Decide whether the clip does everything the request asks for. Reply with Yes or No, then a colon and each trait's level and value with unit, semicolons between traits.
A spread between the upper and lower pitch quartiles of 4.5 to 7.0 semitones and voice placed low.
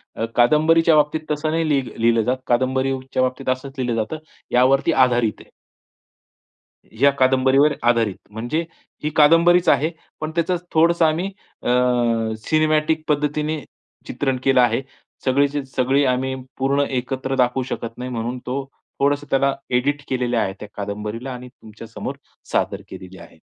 No: average, 3.5 semitones; low, 130 Hz